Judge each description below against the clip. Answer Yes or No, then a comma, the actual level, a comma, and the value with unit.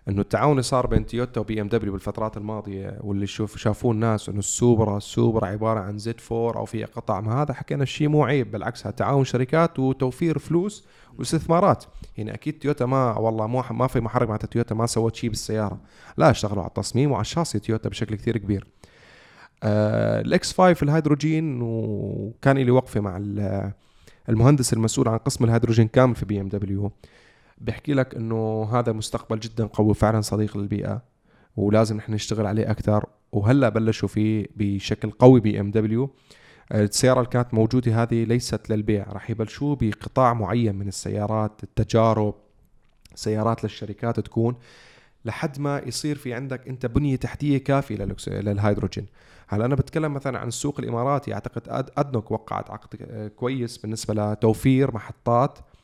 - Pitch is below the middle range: Yes, low, 115 Hz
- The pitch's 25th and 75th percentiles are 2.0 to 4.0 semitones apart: Yes, average, 3.2 semitones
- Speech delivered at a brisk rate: Yes, fast, 155 wpm